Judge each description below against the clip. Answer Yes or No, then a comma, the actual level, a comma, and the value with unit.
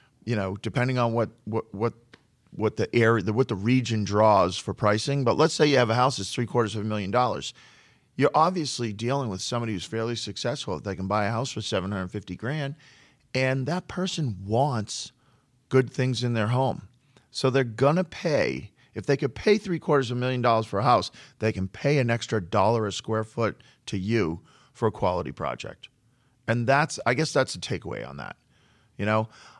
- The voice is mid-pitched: No, low, 120 Hz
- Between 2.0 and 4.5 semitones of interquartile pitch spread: Yes, average, 3.4 semitones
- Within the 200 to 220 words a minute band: Yes, fast, 205 wpm